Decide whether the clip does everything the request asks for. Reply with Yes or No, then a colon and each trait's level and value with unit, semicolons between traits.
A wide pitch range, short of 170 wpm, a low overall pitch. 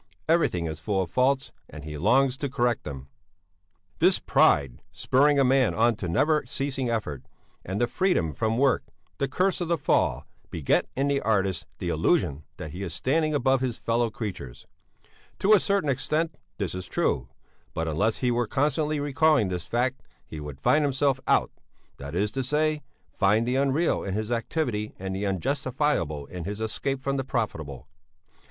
No: wide, 7.2 semitones; average, 175 wpm; low, 120 Hz